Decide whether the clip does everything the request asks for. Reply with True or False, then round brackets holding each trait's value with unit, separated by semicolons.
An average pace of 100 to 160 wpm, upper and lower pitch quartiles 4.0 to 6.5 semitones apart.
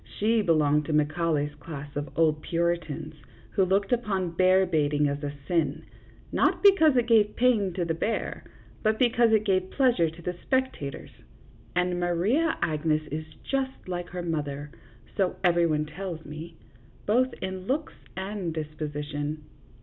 True (155 wpm; 5.2 semitones)